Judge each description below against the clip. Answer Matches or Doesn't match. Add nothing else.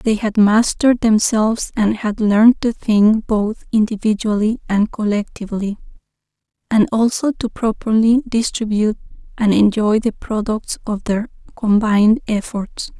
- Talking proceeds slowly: Matches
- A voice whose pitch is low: Doesn't match